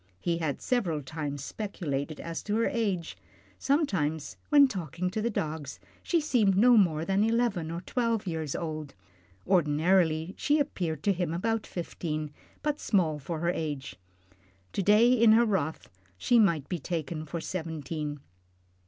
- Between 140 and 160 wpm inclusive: Yes, average, 155 wpm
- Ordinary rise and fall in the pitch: No, wide, 5.7 semitones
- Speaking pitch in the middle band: Yes, medium, 170 Hz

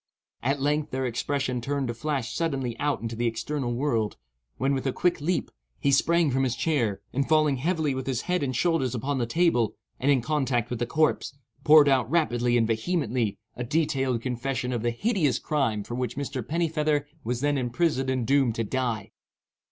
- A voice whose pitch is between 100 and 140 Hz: Yes, low, 135 Hz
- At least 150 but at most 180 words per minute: No, average, 190 wpm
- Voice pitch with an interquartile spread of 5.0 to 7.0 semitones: No, average, 3.7 semitones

